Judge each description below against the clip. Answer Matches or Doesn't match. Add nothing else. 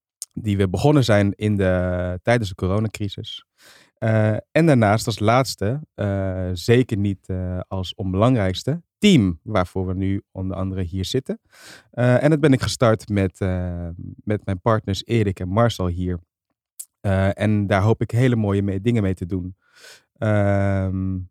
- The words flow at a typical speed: Matches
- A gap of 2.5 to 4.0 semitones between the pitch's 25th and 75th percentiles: Matches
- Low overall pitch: Matches